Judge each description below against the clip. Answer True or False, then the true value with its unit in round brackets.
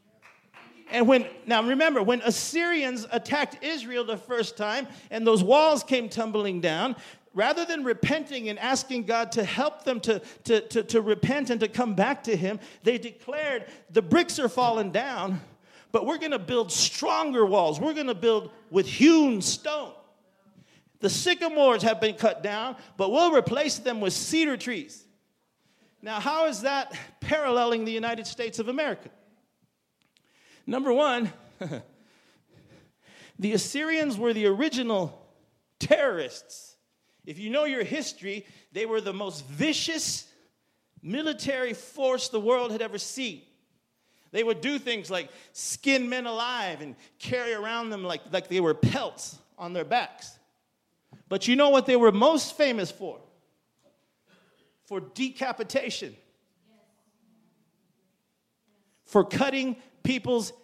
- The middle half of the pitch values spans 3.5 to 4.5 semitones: True (4.2 semitones)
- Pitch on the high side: True (235 Hz)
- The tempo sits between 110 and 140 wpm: True (135 wpm)